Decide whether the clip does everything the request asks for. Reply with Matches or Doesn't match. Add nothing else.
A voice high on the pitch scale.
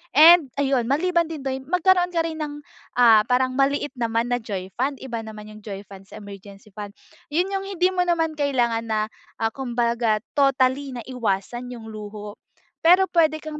Matches